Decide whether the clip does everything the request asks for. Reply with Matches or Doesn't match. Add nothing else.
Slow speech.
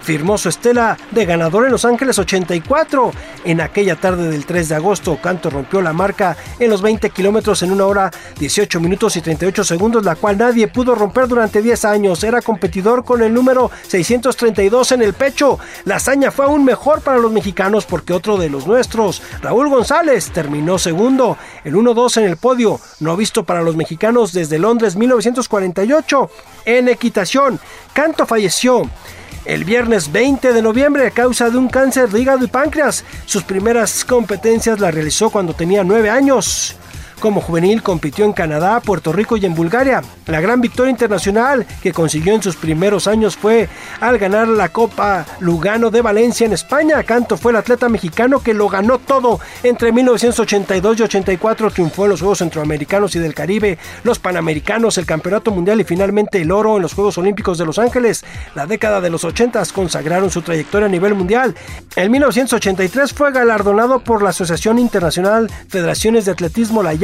Doesn't match